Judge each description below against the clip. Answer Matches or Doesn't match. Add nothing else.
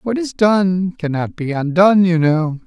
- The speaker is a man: Matches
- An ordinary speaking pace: Matches